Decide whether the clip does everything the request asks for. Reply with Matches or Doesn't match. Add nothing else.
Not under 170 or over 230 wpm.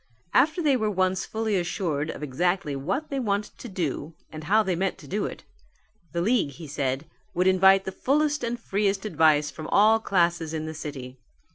Matches